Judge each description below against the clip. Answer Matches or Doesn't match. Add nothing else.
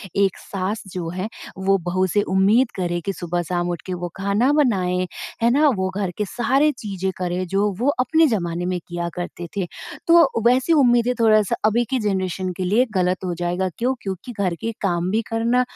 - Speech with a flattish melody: Doesn't match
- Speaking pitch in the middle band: Doesn't match